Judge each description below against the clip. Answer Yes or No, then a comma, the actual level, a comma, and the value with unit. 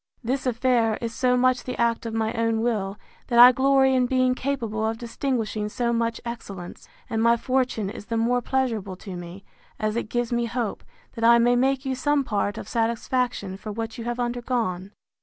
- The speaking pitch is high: Yes, high, 235 Hz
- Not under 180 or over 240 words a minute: Yes, average, 195 wpm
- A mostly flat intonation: Yes, narrow, 2.2 semitones